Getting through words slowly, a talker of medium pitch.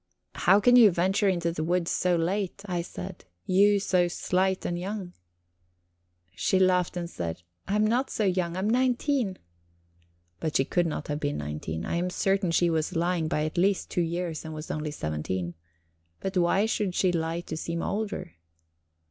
No: average, 180 wpm; medium, 175 Hz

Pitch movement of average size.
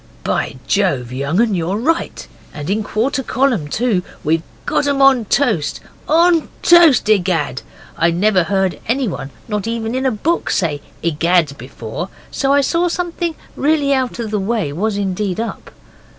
No: wide, 7.8 semitones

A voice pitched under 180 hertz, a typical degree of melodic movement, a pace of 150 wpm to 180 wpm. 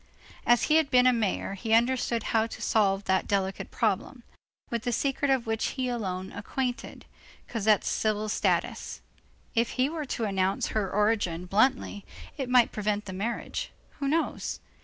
No: high, 225 Hz; average, 3.8 semitones; average, 165 wpm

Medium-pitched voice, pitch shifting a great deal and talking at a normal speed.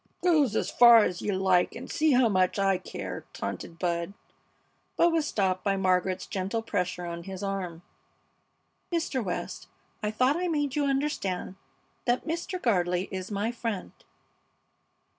No: high, 200 Hz; wide, 6.1 semitones; average, 150 wpm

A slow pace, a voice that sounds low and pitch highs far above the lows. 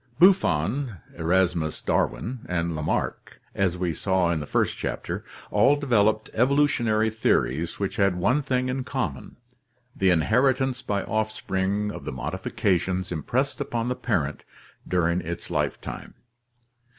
Yes: slow, 130 wpm; low, 100 Hz; wide, 6.4 semitones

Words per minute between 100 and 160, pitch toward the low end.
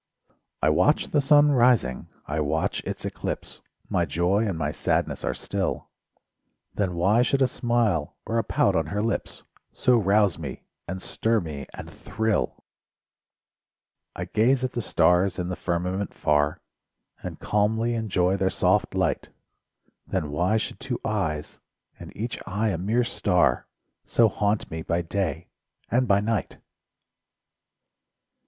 Yes: average, 145 wpm; low, 100 Hz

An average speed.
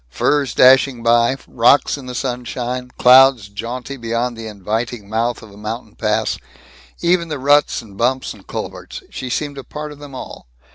Yes: average, 175 wpm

